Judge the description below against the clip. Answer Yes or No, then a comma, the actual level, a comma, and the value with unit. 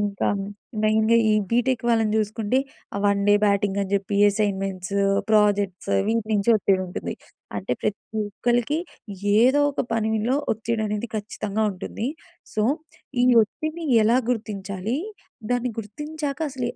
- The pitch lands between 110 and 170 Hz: No, high, 215 Hz